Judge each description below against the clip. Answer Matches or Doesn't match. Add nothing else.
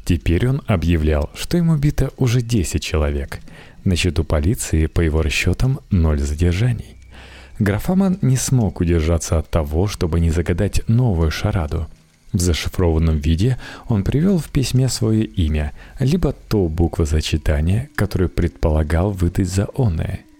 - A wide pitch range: Matches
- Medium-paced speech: Matches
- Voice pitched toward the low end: Matches